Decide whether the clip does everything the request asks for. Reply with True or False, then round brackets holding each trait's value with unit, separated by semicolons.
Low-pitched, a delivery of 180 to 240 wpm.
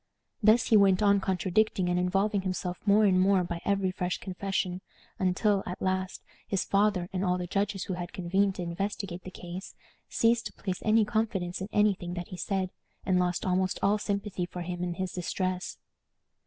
False (185 Hz; 190 wpm)